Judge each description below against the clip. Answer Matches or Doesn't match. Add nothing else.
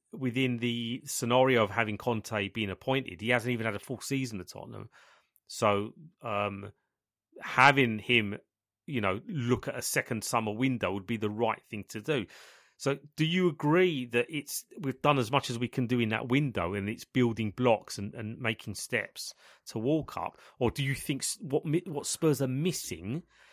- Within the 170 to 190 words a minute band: Matches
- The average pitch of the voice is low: Matches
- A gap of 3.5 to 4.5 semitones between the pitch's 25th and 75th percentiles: Matches